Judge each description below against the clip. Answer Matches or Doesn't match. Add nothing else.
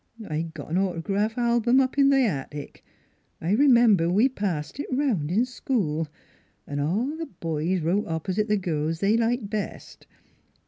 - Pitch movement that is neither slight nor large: Doesn't match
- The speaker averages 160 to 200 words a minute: Matches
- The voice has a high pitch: Matches